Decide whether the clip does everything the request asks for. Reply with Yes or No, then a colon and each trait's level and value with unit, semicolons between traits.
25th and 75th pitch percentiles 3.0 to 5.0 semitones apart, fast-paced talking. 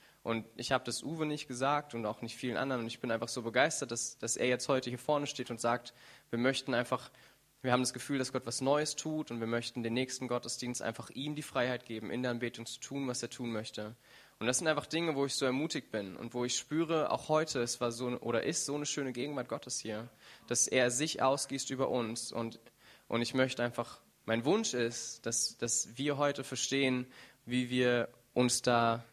No: narrow, 2.4 semitones; fast, 225 wpm